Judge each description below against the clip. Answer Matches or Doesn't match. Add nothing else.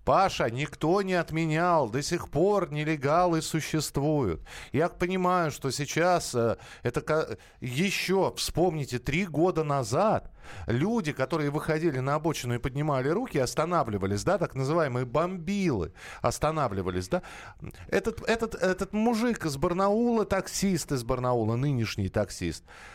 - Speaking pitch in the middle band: Matches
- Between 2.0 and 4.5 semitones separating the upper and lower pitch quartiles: Doesn't match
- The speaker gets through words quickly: Doesn't match